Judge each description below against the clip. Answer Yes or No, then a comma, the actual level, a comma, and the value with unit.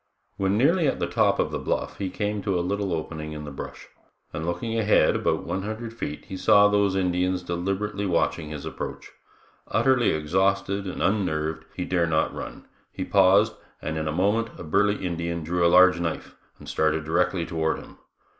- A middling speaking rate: Yes, average, 190 wpm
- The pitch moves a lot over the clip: No, average, 3.7 semitones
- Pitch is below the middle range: Yes, very low, 90 Hz